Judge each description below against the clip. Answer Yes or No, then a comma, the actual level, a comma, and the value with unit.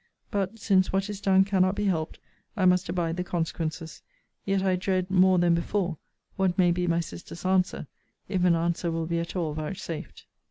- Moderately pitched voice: Yes, medium, 180 Hz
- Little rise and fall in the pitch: Yes, narrow, 2.1 semitones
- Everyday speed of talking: Yes, average, 190 wpm